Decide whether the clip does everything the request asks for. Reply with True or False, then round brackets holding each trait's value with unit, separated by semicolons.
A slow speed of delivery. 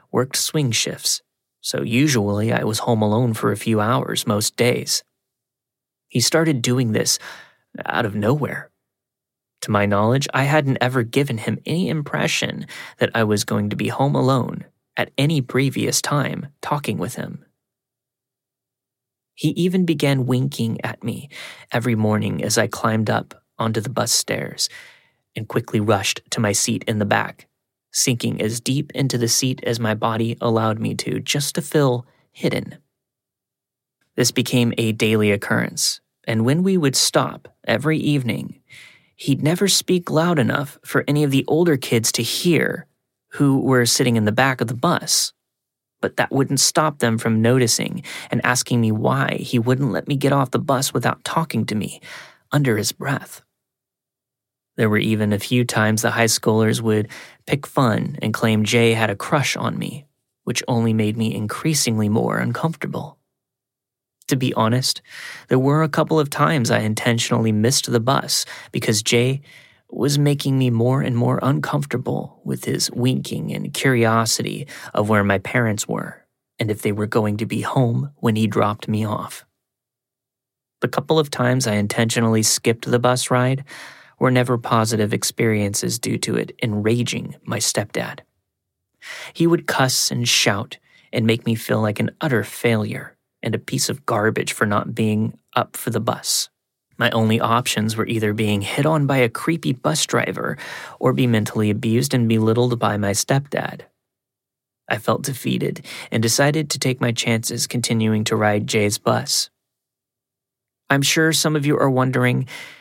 False (165 wpm)